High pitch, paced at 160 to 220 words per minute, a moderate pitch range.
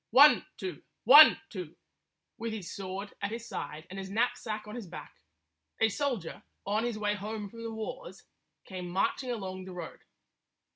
Yes: high, 210 Hz; average, 165 wpm; average, 3.5 semitones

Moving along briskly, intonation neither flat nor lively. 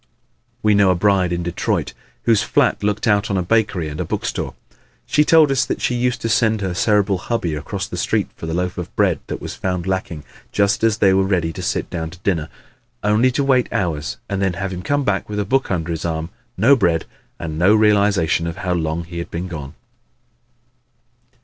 Yes: fast, 215 wpm; average, 3.9 semitones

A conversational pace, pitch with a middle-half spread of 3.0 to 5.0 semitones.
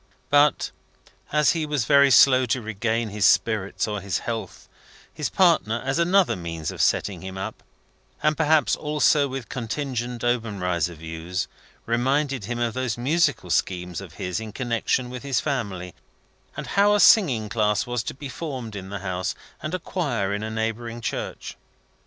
No: average, 165 wpm; wide, 5.6 semitones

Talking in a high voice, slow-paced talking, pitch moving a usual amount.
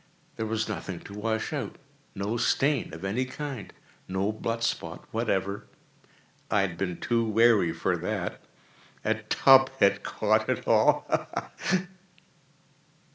No: low, 110 Hz; slow, 120 wpm; average, 3.4 semitones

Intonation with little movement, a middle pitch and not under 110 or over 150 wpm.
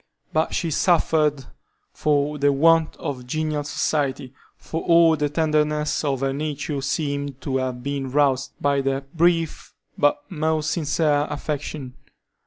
Yes: narrow, 2.1 semitones; medium, 145 Hz; slow, 135 wpm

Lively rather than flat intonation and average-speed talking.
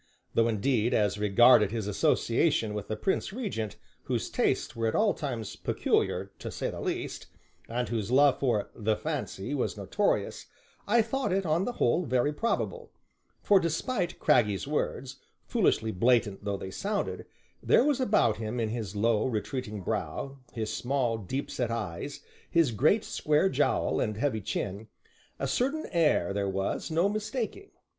Yes: wide, 7.7 semitones; average, 160 wpm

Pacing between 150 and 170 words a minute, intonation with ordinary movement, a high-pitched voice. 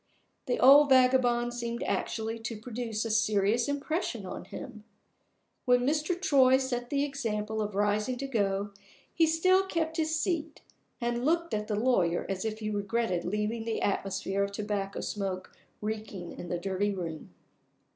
Yes: average, 155 wpm; average, 4.4 semitones; high, 230 Hz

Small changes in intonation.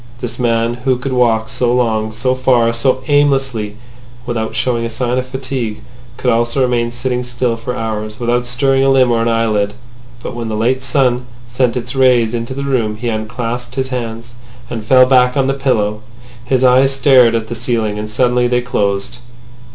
Yes: narrow, 2.0 semitones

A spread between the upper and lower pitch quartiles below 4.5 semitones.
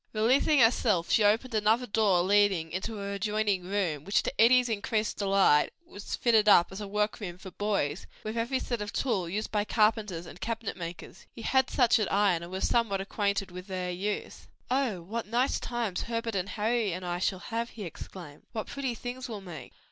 Yes: average, 3.6 semitones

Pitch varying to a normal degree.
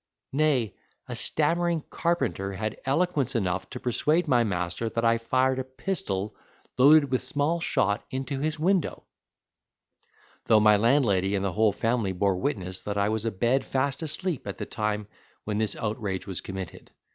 No: wide, 6.0 semitones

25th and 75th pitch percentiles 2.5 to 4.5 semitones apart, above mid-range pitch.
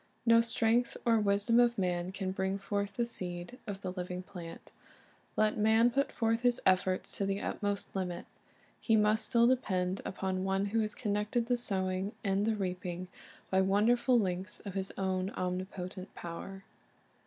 Yes: average, 3.2 semitones; high, 200 Hz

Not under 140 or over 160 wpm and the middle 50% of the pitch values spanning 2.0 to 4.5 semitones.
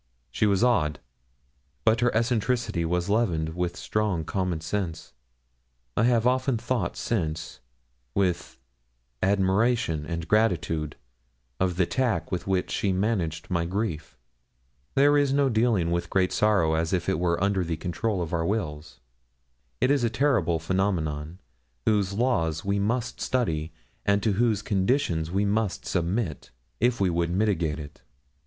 No: average, 150 wpm; average, 5.1 semitones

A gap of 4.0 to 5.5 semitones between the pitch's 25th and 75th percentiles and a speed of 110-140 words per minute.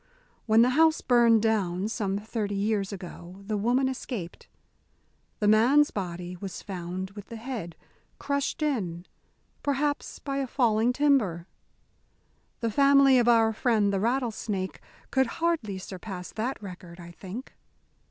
Yes: average, 5.2 semitones; slow, 135 wpm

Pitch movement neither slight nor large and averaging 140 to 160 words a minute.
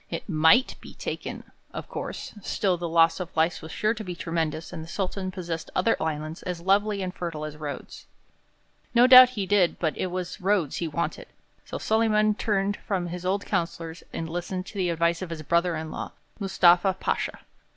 No: average, 3.1 semitones; average, 195 wpm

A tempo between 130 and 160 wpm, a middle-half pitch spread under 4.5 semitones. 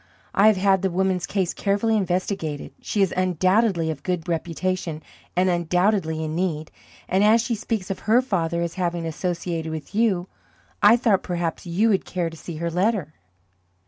No: average, 175 wpm; average, 2.9 semitones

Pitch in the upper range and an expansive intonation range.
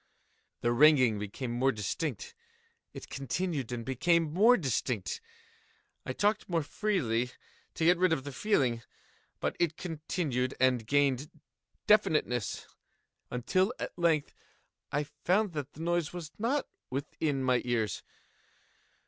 No: medium, 150 Hz; wide, 5.9 semitones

